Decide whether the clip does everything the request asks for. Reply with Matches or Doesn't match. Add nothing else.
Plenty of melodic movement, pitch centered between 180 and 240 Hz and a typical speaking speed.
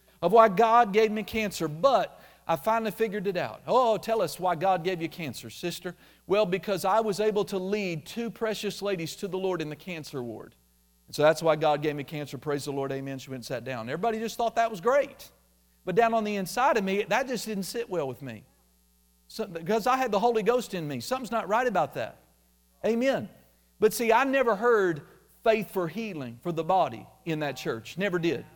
Doesn't match